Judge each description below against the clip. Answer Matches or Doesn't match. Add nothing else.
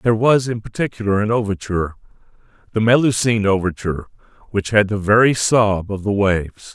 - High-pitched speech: Doesn't match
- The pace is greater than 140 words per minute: Doesn't match